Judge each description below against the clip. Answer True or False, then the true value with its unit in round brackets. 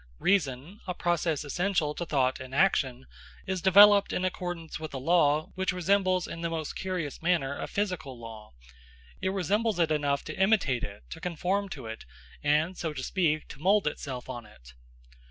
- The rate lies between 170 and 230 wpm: True (175 wpm)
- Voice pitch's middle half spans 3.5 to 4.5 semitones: False (4.9 semitones)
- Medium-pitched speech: True (165 Hz)